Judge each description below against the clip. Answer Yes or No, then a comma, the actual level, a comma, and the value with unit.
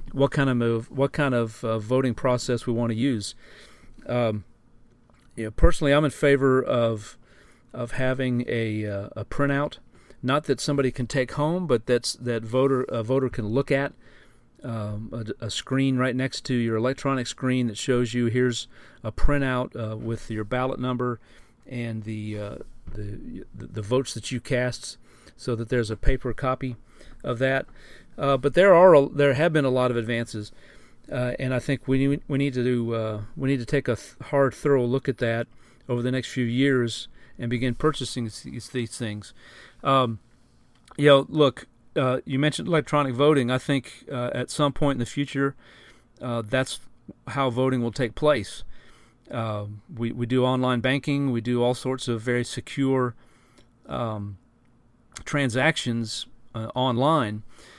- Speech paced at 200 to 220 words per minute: No, average, 175 wpm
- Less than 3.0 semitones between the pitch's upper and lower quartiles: Yes, narrow, 2.5 semitones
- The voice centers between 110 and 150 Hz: Yes, low, 125 Hz